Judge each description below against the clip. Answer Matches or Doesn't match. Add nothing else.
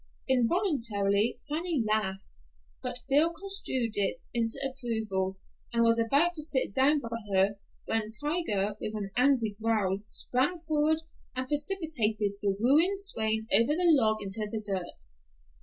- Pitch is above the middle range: Matches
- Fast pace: Doesn't match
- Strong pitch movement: Matches